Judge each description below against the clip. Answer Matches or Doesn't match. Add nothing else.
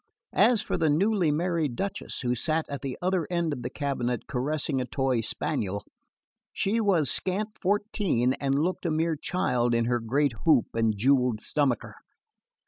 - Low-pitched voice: Doesn't match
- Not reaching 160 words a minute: Doesn't match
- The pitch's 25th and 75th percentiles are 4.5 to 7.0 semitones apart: Matches